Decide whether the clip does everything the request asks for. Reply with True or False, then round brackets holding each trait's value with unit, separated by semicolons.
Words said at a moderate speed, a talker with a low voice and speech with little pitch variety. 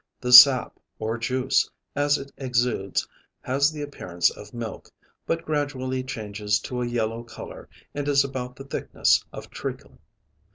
False (150 wpm; 125 Hz; 3.1 semitones)